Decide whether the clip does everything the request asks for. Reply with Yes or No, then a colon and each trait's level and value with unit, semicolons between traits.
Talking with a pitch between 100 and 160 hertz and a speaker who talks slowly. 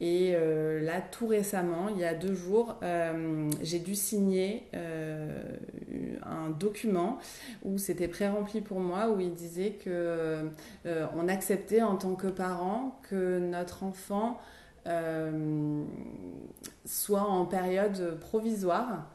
No: medium, 185 Hz; slow, 125 wpm